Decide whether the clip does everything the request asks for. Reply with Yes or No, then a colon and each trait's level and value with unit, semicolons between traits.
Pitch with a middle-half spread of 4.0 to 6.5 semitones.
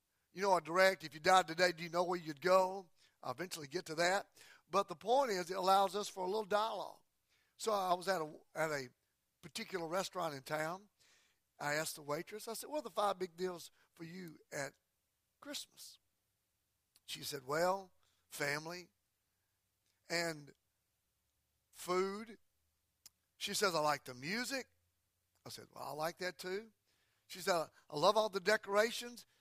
Yes: average, 4.4 semitones